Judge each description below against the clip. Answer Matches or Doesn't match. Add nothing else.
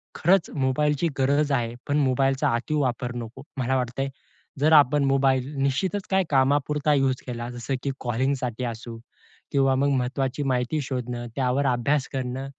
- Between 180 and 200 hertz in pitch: Doesn't match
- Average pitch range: Doesn't match